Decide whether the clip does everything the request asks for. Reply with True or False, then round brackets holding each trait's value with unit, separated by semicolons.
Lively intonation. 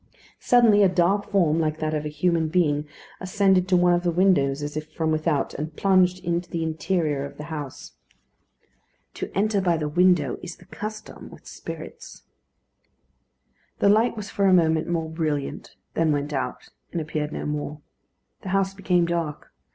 False (3.5 semitones)